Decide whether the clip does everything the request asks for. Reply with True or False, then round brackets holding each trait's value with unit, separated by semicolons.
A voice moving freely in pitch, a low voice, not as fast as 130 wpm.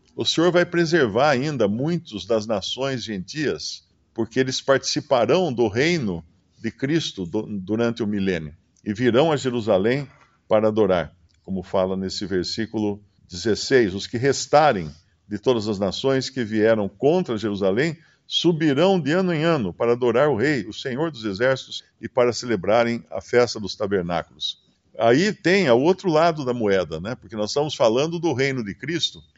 False (6.3 semitones; 115 Hz; 160 wpm)